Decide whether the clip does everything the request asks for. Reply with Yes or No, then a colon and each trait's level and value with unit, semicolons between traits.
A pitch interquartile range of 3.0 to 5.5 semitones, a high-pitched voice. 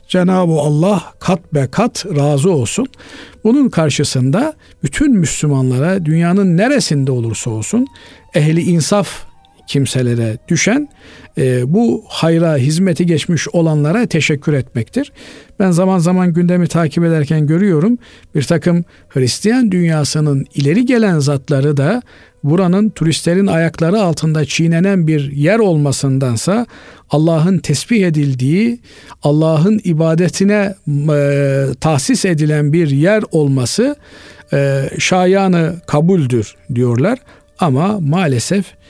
No: average, 4.7 semitones; medium, 165 Hz